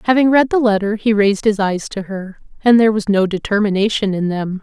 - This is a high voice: Yes, high, 210 Hz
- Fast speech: Yes, fast, 220 wpm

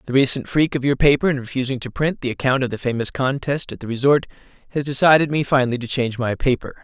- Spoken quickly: Yes, fast, 235 wpm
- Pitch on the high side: No, low, 130 Hz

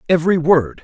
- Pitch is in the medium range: Yes, medium, 165 Hz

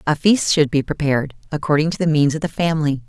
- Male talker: No, female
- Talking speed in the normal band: No, fast, 235 wpm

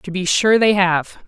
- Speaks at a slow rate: No, fast, 235 wpm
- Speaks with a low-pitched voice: No, high, 190 Hz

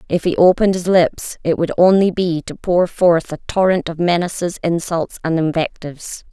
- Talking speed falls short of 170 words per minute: No, average, 180 wpm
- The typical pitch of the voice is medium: Yes, medium, 170 Hz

